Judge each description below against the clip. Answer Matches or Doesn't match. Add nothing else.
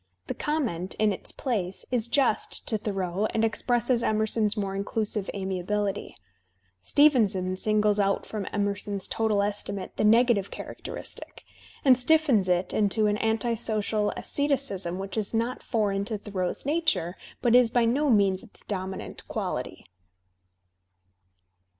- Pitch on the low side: Doesn't match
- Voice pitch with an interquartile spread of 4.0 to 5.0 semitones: Doesn't match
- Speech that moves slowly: Matches